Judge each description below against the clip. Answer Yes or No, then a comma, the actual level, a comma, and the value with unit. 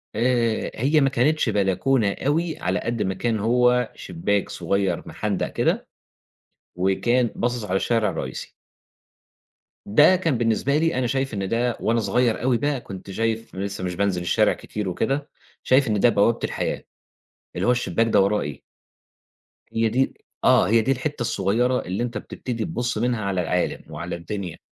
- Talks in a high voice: No, low, 115 Hz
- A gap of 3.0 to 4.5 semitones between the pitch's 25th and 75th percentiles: Yes, average, 4.1 semitones